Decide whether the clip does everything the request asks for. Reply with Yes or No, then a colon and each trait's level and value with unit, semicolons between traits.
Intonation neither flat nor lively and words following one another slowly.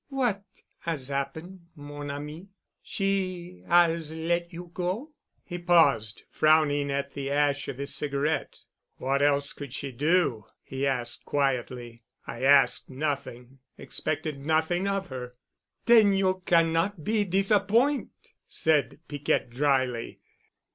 Yes: average, 4.3 semitones; slow, 120 wpm